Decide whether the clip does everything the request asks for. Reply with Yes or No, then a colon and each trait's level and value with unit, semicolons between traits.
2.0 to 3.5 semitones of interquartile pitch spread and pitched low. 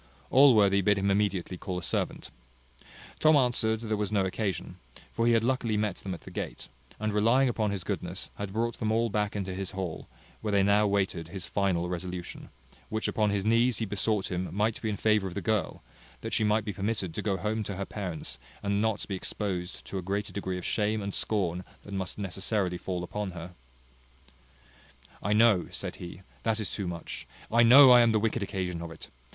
Yes: average, 2.7 semitones; low, 100 Hz